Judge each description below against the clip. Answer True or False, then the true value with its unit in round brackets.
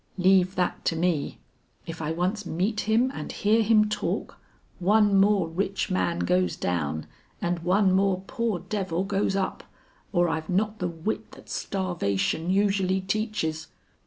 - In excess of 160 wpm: False (150 wpm)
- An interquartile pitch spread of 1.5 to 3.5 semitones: True (3.0 semitones)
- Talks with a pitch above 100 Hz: True (190 Hz)